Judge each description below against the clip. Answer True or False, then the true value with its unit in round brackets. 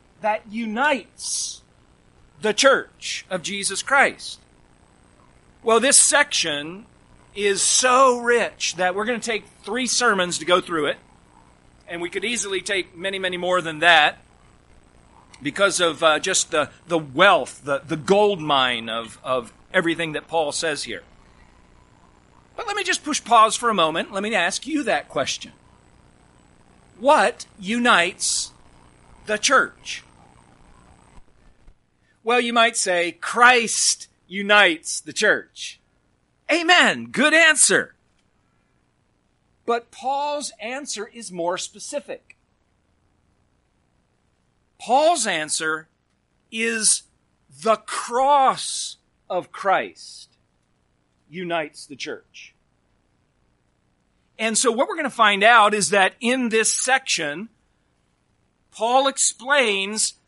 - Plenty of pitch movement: True (6.4 semitones)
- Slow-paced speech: True (110 wpm)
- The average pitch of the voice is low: False (205 Hz)